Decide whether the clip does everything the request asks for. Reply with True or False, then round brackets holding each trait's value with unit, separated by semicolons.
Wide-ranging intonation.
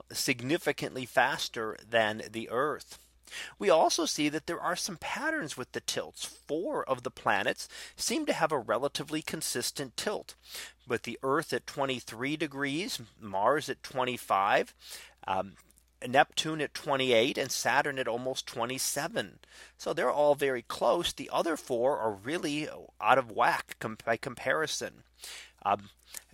False (4.2 semitones)